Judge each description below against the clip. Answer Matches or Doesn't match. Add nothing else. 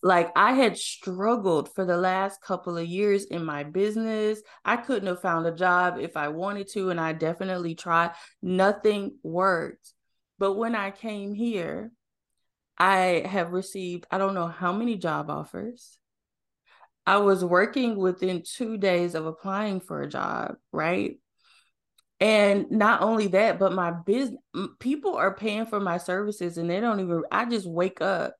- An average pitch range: Matches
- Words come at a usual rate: Matches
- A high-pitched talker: Matches